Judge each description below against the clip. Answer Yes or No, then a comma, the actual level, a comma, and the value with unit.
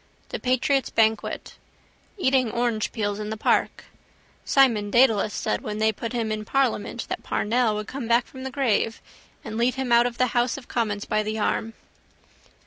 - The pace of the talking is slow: No, average, 175 wpm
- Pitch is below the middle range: No, high, 230 Hz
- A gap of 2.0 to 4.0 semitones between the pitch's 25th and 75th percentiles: Yes, average, 2.8 semitones